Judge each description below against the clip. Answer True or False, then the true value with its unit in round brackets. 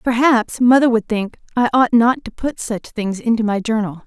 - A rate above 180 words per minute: True (205 wpm)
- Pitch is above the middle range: True (230 Hz)